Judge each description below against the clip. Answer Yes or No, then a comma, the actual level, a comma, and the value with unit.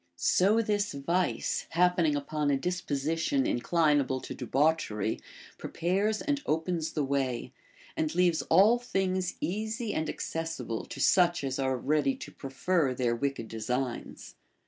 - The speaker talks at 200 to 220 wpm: No, slow, 135 wpm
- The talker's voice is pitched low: No, medium, 160 Hz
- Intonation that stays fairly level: No, average, 5.3 semitones